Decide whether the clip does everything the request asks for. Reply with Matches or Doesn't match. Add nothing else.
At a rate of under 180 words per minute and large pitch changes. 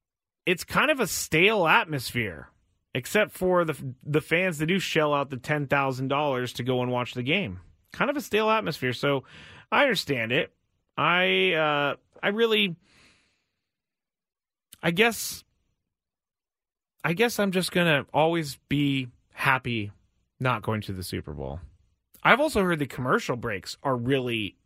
Matches